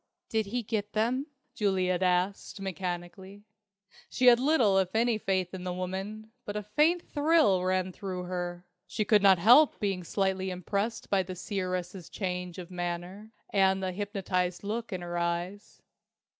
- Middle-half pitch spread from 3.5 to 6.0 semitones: No, average, 2.7 semitones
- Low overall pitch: No, high, 190 Hz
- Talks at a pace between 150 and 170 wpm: Yes, average, 155 wpm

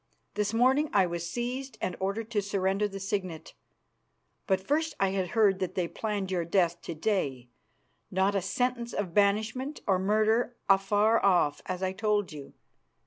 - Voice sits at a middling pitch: No, high, 200 Hz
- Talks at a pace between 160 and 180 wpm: Yes, average, 165 wpm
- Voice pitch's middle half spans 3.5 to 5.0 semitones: No, average, 2.9 semitones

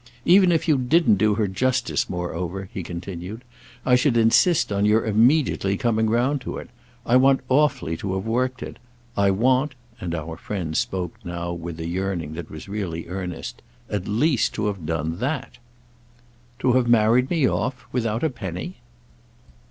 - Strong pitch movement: Yes, wide, 6.1 semitones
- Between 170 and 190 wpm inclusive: No, average, 160 wpm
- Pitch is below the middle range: Yes, low, 110 Hz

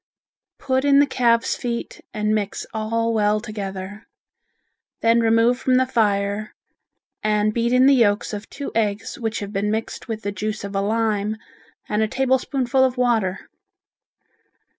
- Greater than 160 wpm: No, average, 155 wpm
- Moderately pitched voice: No, high, 220 Hz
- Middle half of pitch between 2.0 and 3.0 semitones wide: Yes, average, 2.7 semitones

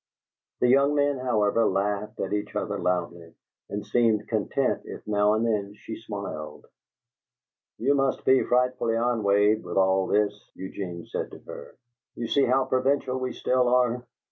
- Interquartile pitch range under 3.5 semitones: No, average, 3.8 semitones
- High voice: No, low, 110 Hz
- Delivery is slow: No, average, 155 wpm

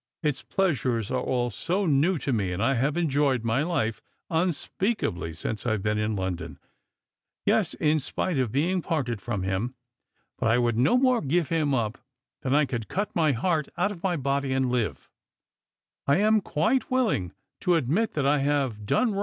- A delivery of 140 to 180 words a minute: No, average, 190 wpm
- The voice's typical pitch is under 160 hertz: Yes, medium, 140 Hz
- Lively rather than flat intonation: Yes, wide, 6.5 semitones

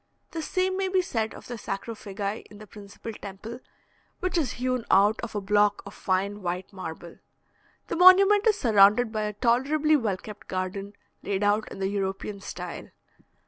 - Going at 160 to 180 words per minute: Yes, average, 175 wpm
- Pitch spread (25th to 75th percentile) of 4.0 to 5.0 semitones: Yes, average, 4.3 semitones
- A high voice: Yes, high, 210 Hz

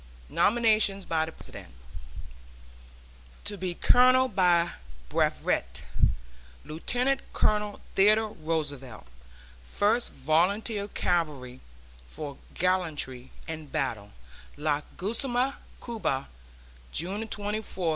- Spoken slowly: Yes, slow, 85 wpm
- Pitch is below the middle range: No, medium, 180 Hz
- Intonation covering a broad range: Yes, wide, 6.1 semitones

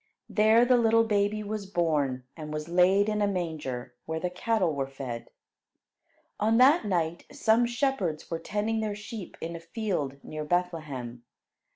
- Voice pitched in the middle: Yes, medium, 180 Hz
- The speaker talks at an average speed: Yes, average, 160 wpm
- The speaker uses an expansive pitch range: Yes, wide, 5.9 semitones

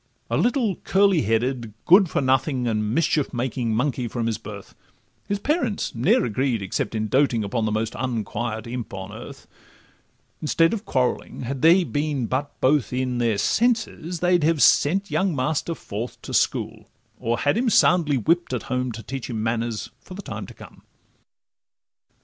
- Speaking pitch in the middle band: No, low, 130 Hz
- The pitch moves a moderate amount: No, wide, 6.3 semitones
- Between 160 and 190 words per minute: Yes, average, 170 wpm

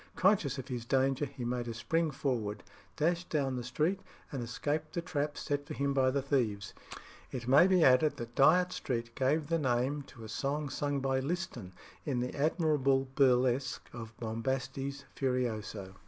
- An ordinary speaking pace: Yes, average, 170 wpm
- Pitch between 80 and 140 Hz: Yes, low, 135 Hz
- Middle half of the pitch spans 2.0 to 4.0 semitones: Yes, average, 3.2 semitones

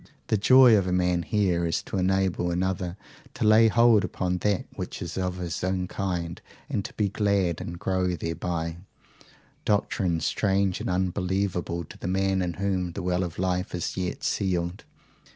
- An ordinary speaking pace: Yes, average, 170 wpm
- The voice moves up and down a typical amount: No, narrow, 1.9 semitones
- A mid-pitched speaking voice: No, very low, 90 Hz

